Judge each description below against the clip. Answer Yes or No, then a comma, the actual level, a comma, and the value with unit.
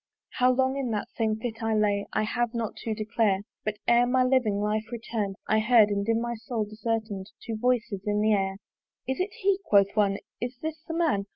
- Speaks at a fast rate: Yes, fast, 210 wpm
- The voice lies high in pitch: Yes, high, 225 Hz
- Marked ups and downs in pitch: No, average, 2.8 semitones